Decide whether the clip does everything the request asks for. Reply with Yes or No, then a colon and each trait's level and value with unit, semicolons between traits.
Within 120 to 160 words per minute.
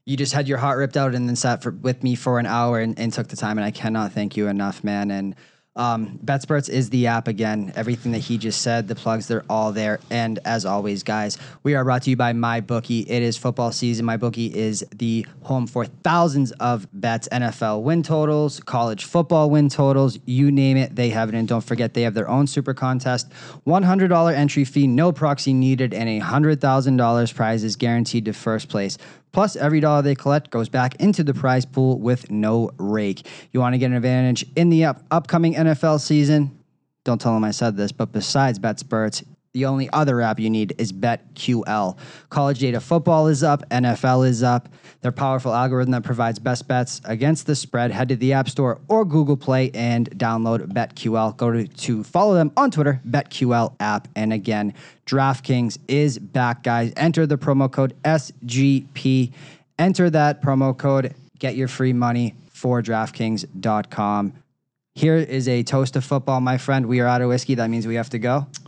No: average, 200 wpm